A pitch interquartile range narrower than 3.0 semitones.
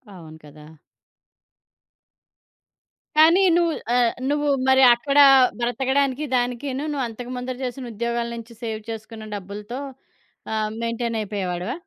No: average, 3.3 semitones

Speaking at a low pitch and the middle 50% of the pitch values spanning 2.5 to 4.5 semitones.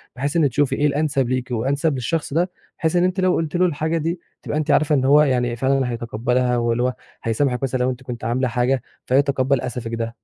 Yes: low, 130 Hz; average, 3.5 semitones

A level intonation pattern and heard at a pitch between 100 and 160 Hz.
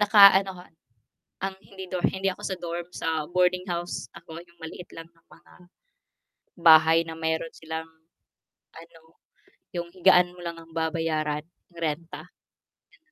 No: narrow, 1.7 semitones; medium, 170 Hz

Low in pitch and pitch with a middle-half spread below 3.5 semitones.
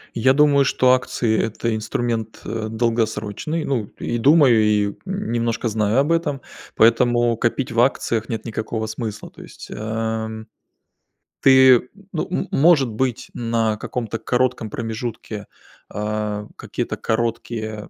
Yes: low, 115 Hz; narrow, 2.5 semitones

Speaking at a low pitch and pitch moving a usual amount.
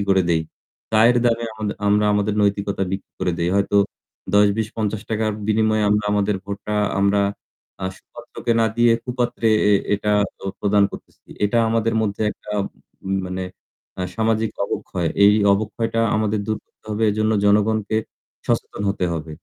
No: low, 105 Hz; narrow, 1.7 semitones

